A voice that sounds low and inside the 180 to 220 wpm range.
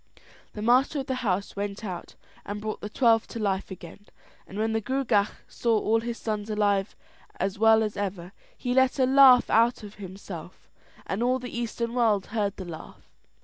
No: high, 215 Hz; average, 190 wpm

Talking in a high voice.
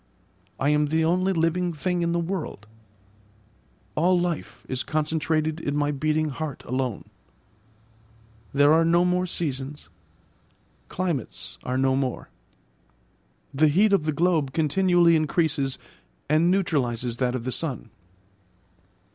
No: medium, 155 Hz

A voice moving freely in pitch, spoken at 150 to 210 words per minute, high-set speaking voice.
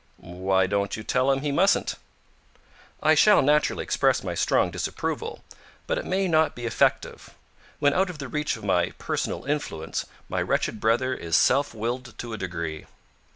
No: wide, 7.1 semitones; average, 170 wpm; low, 125 Hz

